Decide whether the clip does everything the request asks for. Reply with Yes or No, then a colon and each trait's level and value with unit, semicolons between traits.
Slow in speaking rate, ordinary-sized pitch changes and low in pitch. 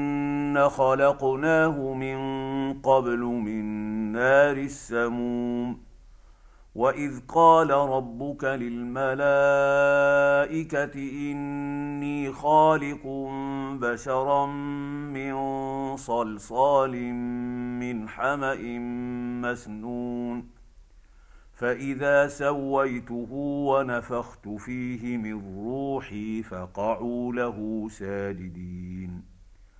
Yes: slow, 55 wpm; average, 3.0 semitones; low, 130 Hz